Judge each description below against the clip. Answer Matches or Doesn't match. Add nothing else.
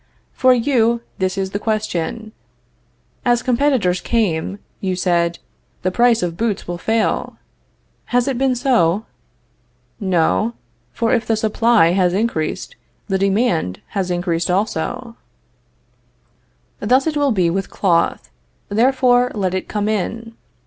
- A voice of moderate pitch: Doesn't match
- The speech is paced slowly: Matches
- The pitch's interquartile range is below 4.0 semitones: Doesn't match